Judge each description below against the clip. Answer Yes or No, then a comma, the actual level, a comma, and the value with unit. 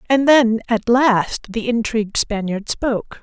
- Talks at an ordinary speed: Yes, average, 150 wpm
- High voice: Yes, high, 230 Hz